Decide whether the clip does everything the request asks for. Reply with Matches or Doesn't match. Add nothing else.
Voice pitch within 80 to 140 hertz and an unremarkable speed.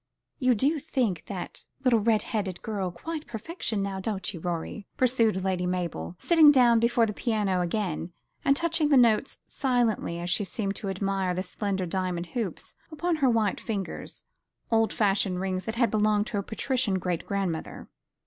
Doesn't match